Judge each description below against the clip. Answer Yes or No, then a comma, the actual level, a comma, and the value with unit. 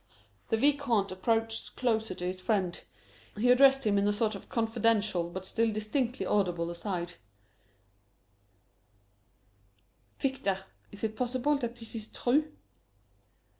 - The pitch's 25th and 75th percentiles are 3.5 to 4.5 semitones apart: Yes, average, 3.8 semitones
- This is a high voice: Yes, high, 220 Hz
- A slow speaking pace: Yes, slow, 125 wpm